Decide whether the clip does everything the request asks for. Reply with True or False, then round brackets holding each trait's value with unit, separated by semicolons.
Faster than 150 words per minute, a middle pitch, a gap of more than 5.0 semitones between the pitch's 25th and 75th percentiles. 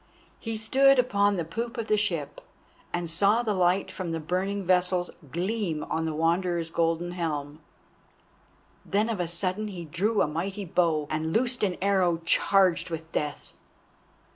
False (160 wpm; 180 Hz; 3.7 semitones)